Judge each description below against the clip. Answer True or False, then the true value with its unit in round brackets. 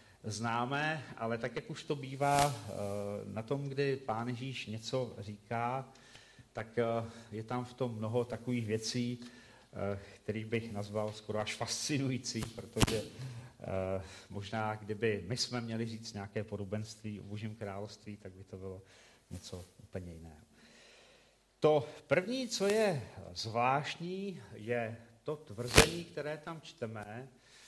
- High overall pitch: False (115 Hz)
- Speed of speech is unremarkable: True (125 wpm)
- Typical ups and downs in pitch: True (3.7 semitones)